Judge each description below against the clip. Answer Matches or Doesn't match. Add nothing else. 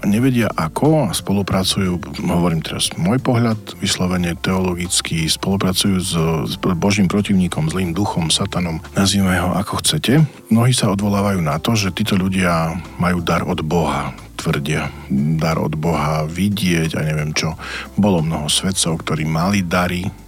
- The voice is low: Matches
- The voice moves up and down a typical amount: Matches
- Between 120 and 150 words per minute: Matches